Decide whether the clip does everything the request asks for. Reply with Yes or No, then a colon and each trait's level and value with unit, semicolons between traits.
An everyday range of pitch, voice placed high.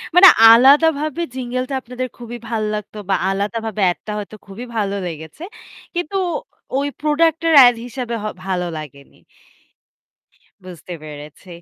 No: wide, 5.9 semitones; high, 230 Hz